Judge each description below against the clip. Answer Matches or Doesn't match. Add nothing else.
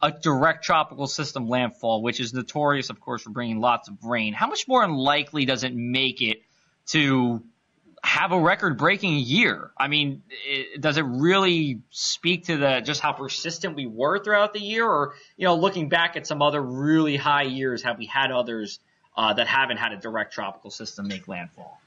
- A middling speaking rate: Matches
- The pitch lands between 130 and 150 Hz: Matches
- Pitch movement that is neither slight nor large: Matches